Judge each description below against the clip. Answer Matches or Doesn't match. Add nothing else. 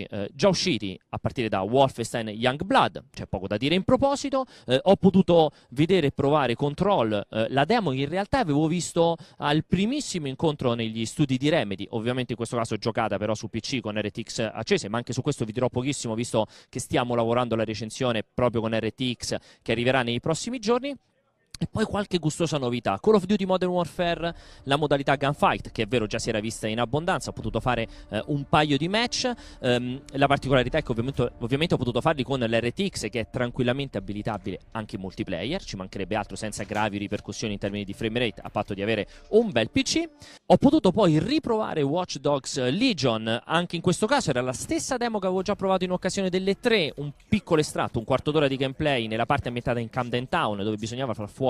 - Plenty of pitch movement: Matches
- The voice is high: Doesn't match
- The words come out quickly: Matches